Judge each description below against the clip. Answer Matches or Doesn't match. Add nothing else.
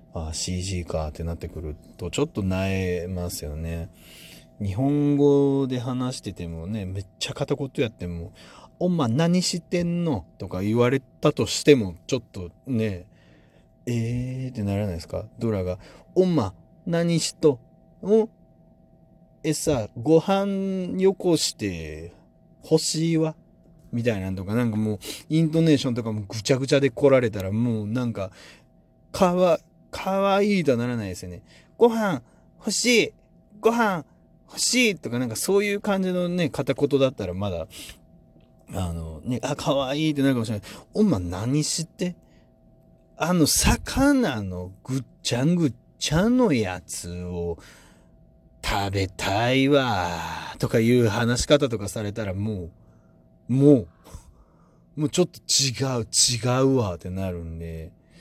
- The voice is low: Matches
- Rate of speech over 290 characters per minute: Doesn't match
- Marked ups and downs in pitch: Matches